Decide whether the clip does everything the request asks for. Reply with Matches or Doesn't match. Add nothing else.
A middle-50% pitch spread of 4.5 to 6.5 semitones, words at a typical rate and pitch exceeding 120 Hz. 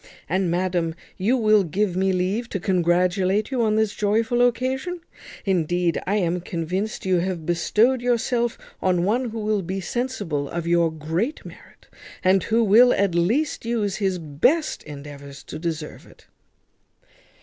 Matches